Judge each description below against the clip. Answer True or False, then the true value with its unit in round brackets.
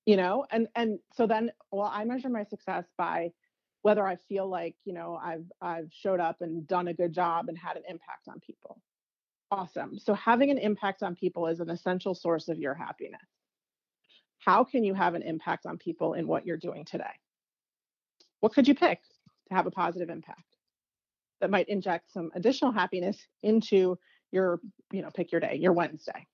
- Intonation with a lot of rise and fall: False (3.5 semitones)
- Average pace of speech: True (190 wpm)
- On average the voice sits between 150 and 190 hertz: True (185 Hz)